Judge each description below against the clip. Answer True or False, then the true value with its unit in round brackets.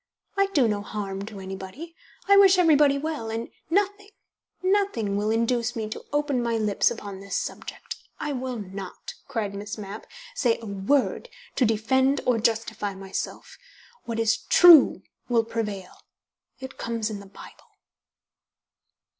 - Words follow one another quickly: False (145 wpm)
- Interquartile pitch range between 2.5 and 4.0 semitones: False (5.3 semitones)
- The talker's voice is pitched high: True (230 Hz)